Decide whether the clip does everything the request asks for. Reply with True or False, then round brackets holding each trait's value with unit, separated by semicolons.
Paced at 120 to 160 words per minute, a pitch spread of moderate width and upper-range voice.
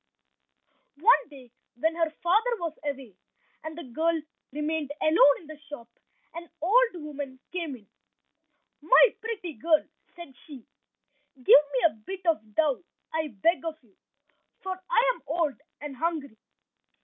True (145 wpm; 3.8 semitones; 315 Hz)